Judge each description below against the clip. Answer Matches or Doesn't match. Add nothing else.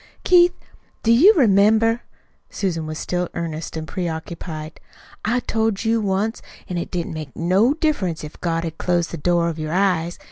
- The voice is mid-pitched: Matches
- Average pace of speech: Matches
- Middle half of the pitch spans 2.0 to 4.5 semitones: Doesn't match